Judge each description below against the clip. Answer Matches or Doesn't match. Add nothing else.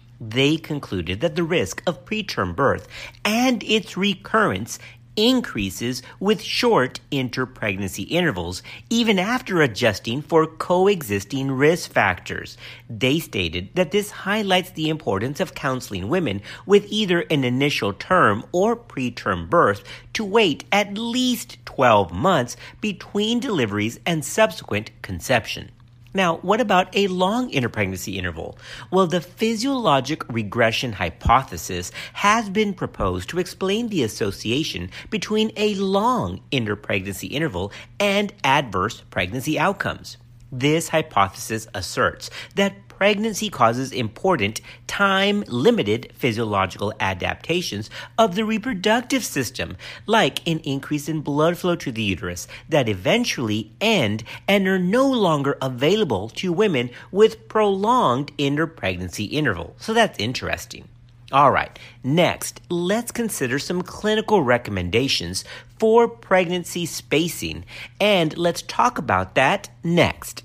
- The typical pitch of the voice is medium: Matches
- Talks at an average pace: Doesn't match